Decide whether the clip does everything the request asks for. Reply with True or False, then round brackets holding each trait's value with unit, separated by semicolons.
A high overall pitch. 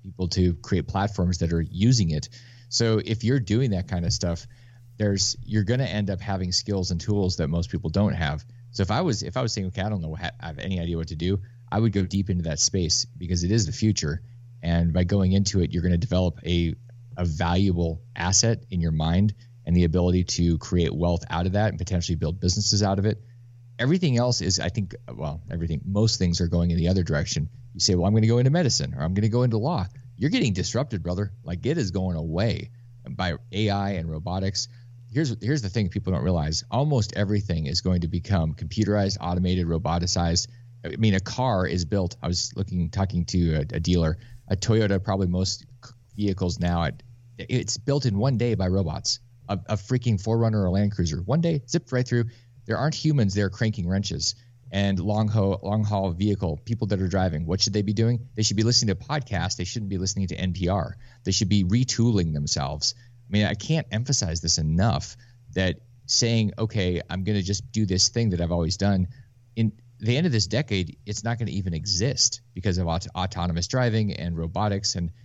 False (100 Hz)